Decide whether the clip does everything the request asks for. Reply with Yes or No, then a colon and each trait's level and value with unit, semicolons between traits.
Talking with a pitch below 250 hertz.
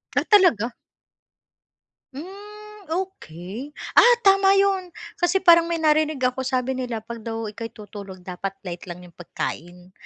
No: very high, 260 Hz